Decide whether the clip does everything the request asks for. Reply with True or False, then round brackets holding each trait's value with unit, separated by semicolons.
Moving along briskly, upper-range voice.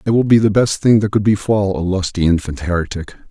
False (235 wpm; 100 Hz)